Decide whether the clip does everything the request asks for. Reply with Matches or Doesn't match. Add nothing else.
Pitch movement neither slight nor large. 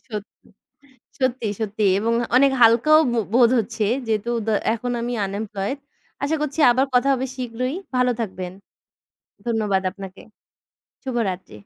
Matches